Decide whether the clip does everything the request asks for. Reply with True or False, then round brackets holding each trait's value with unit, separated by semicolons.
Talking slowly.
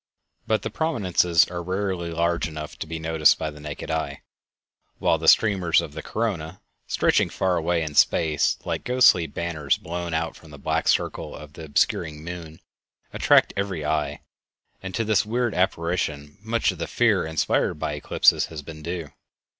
False (170 wpm)